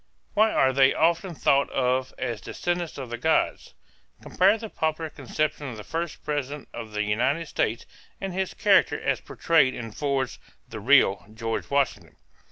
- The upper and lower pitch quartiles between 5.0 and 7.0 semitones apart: Yes, wide, 5.4 semitones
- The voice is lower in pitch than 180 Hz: Yes, medium, 140 Hz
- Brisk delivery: No, average, 165 wpm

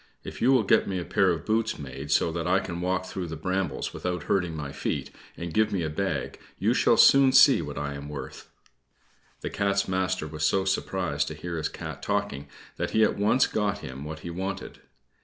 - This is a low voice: Yes, very low, 90 Hz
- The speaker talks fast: Yes, fast, 215 wpm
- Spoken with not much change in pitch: No, average, 4.3 semitones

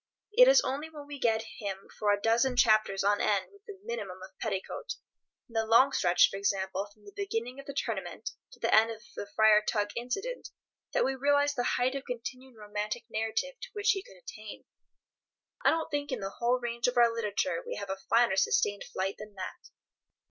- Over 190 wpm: Yes, average, 200 wpm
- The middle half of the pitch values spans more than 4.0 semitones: Yes, average, 5.1 semitones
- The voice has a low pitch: No, high, 230 Hz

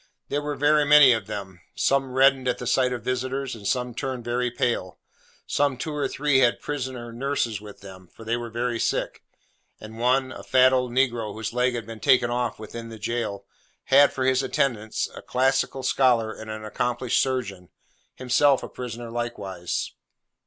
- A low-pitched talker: Yes, low, 125 Hz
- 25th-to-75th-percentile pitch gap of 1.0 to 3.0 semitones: Yes, narrow, 2.6 semitones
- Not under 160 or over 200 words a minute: Yes, average, 180 wpm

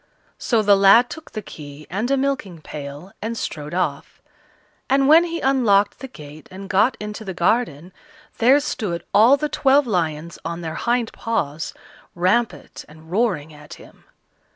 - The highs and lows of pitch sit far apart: Yes, wide, 6.9 semitones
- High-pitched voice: Yes, high, 200 Hz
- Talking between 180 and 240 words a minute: No, average, 160 wpm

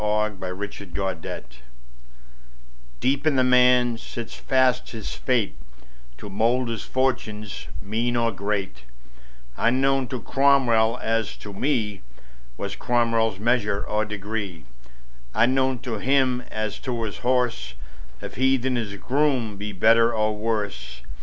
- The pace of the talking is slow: Yes, slow, 130 wpm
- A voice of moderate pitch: No, low, 115 Hz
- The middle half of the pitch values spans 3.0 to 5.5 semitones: Yes, average, 3.5 semitones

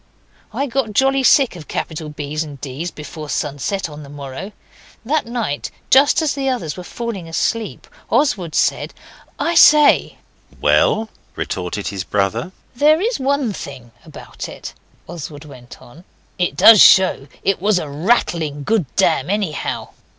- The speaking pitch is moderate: Yes, medium, 175 Hz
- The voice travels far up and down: Yes, wide, 8.6 semitones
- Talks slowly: No, average, 150 wpm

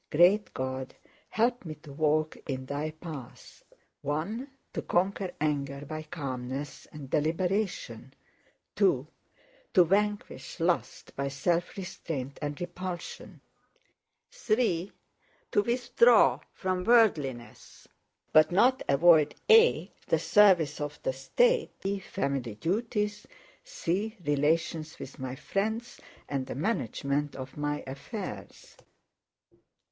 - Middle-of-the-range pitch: Yes, medium, 160 Hz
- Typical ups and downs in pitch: No, wide, 6.3 semitones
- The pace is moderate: No, slow, 110 wpm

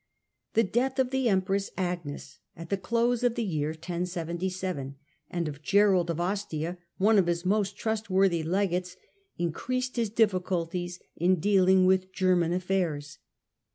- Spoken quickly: No, average, 145 wpm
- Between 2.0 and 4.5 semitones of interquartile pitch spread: Yes, average, 2.9 semitones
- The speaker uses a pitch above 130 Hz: Yes, medium, 185 Hz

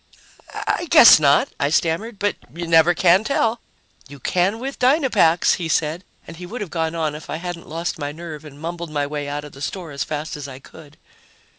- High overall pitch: No, medium, 165 Hz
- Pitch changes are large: No, average, 3.4 semitones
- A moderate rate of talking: No, fast, 210 wpm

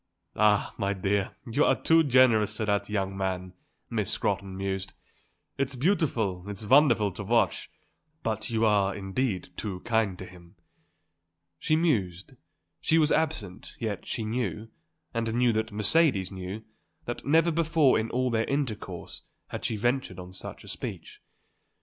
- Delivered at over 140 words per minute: Yes, average, 150 wpm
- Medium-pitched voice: No, low, 110 Hz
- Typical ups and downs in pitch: Yes, average, 4.8 semitones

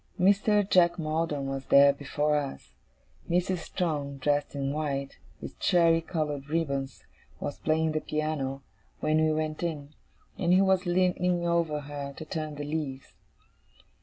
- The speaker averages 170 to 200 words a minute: No, average, 145 wpm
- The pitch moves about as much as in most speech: Yes, average, 3.2 semitones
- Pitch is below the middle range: No, medium, 155 Hz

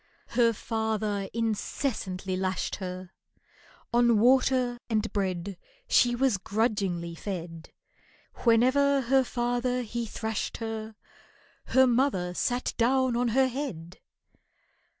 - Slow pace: Yes, slow, 105 wpm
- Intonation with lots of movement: No, average, 4.3 semitones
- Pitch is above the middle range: Yes, high, 230 Hz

